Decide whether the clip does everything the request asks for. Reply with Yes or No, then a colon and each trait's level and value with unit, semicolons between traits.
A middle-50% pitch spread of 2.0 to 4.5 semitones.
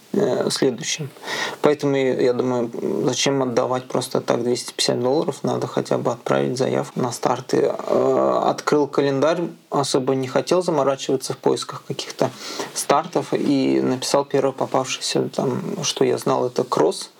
No: average, 4.9 semitones